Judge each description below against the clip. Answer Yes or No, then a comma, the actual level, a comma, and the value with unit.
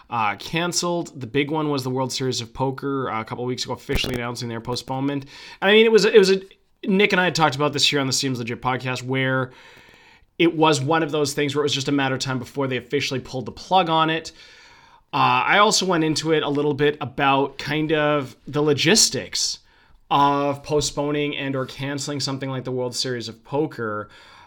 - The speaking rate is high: Yes, fast, 225 wpm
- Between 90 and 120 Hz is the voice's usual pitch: No, medium, 140 Hz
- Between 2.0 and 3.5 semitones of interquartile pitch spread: Yes, average, 3.2 semitones